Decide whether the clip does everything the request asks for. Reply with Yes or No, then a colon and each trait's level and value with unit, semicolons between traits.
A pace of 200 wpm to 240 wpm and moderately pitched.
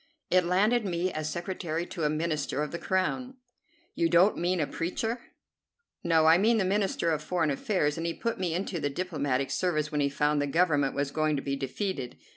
Yes: fast, 205 wpm; medium, 165 Hz